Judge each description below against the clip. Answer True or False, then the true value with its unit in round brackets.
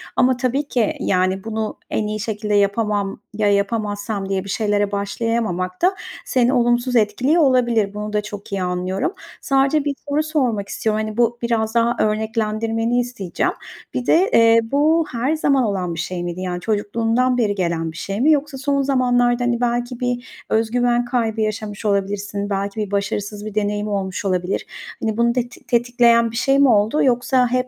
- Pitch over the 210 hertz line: True (225 Hz)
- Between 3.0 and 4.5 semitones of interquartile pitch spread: True (3.4 semitones)